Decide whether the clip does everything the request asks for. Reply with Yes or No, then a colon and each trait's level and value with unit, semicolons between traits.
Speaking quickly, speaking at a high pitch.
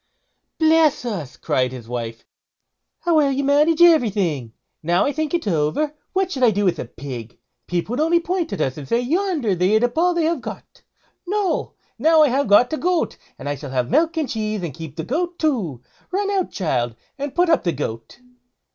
Yes: fast, 210 wpm; high, 245 Hz